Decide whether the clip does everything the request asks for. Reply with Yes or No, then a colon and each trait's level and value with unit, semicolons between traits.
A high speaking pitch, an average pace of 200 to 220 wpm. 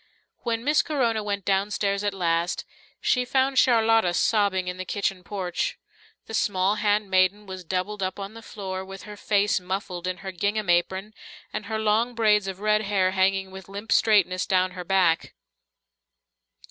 No: high, 200 Hz; average, 165 wpm